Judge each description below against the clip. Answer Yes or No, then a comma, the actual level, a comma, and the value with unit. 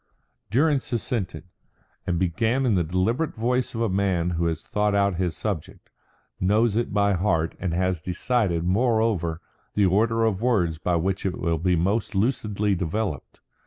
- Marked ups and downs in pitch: No, average, 4.3 semitones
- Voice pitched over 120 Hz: No, low, 100 Hz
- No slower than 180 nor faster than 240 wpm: No, average, 160 wpm